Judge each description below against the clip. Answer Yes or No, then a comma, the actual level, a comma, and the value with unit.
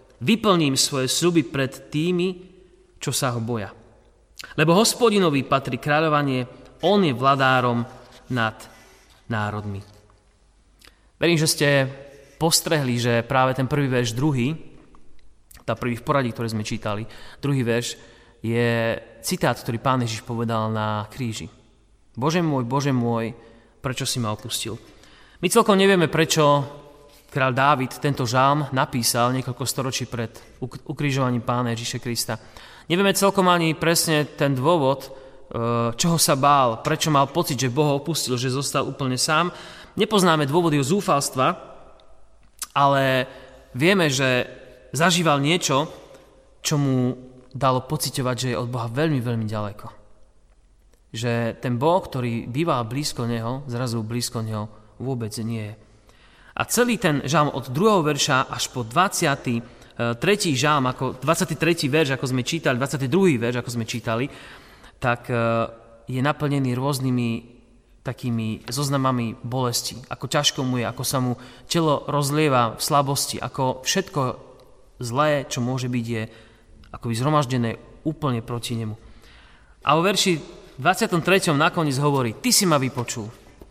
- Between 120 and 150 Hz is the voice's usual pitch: Yes, low, 130 Hz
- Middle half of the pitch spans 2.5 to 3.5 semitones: No, average, 4.1 semitones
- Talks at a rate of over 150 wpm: No, average, 130 wpm